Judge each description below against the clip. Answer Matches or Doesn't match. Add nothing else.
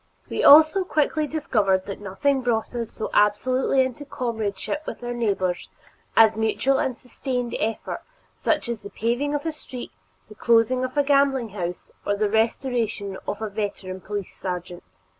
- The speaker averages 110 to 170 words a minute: Matches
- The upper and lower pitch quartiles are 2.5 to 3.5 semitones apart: Doesn't match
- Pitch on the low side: Doesn't match